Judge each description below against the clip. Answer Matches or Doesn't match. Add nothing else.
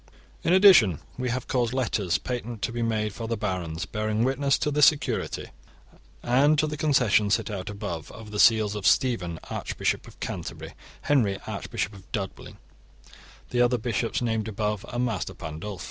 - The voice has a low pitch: Matches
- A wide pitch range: Doesn't match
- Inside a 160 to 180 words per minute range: Matches